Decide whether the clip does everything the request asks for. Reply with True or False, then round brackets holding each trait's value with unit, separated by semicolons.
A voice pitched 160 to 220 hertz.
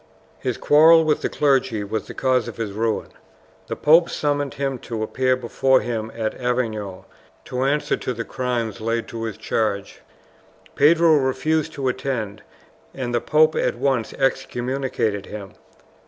False (125 Hz)